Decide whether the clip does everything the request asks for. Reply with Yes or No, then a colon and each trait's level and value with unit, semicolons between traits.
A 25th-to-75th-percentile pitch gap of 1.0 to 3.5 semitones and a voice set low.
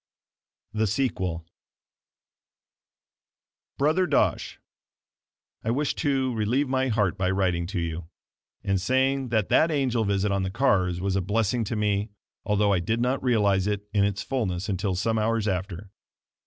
No: average, 4.6 semitones; low, 105 Hz